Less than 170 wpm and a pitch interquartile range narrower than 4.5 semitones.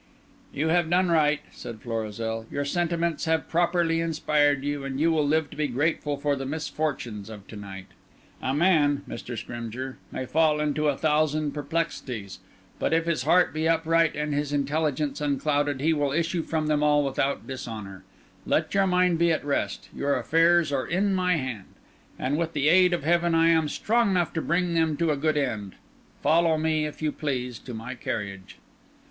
No: average, 185 wpm; average, 3.4 semitones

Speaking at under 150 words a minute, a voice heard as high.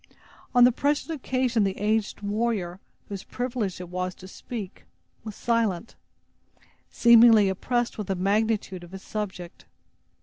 Yes: slow, 135 wpm; high, 210 Hz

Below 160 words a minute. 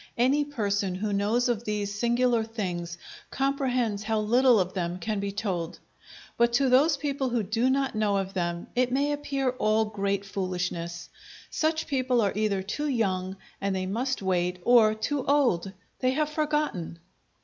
No: average, 165 wpm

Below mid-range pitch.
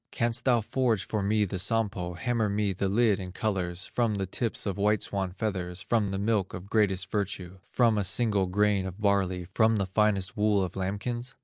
Yes: low, 100 Hz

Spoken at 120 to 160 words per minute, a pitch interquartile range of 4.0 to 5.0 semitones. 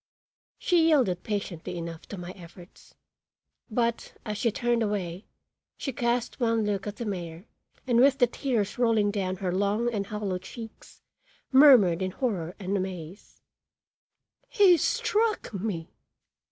Yes: average, 140 wpm; average, 4.5 semitones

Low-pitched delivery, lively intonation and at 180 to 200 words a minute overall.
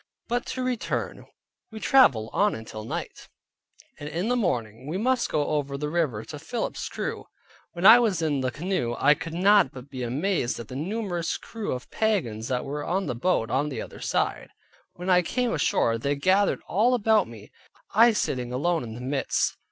No: medium, 155 Hz; wide, 8.1 semitones; average, 190 wpm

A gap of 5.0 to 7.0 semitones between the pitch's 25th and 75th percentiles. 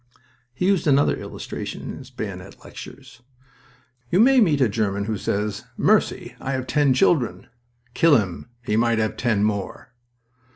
Yes: wide, 5.5 semitones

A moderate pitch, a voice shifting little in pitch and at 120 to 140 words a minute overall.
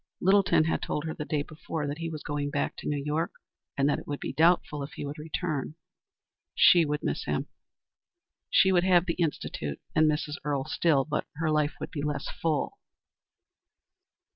No: medium, 150 Hz; narrow, 2.2 semitones; average, 185 wpm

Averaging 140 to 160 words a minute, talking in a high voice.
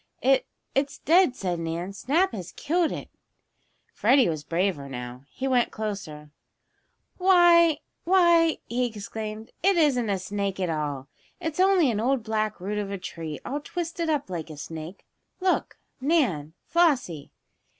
Yes: average, 150 wpm; high, 220 Hz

